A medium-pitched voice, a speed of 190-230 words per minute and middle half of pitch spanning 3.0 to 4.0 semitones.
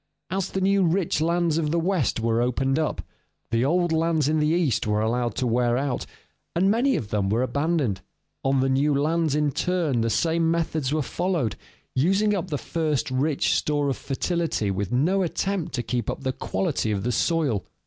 No: medium, 150 Hz; average, 195 wpm; wide, 5.4 semitones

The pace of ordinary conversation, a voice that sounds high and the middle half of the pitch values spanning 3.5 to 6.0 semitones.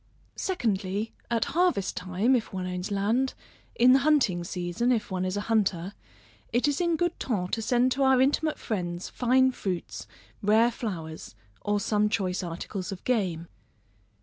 Yes: average, 160 wpm; high, 210 Hz; wide, 5.5 semitones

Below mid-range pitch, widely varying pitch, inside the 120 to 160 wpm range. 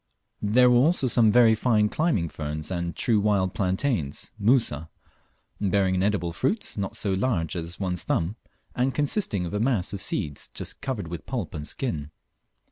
No: low, 100 Hz; wide, 6.0 semitones; average, 170 wpm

